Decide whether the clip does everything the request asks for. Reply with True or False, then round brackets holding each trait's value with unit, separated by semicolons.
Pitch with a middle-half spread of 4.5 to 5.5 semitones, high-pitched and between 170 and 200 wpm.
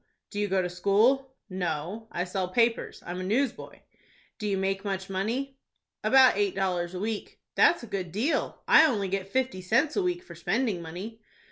True (4.8 semitones; 200 Hz; 190 wpm)